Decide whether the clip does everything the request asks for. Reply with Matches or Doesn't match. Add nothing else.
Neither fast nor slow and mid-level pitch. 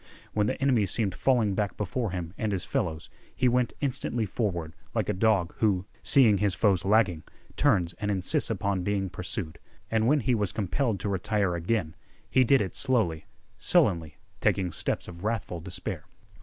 Doesn't match